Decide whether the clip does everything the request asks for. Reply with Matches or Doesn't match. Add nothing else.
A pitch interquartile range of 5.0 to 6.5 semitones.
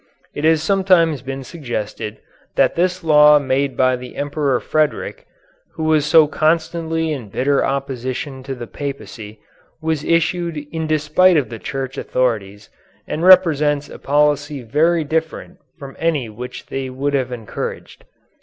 Doesn't match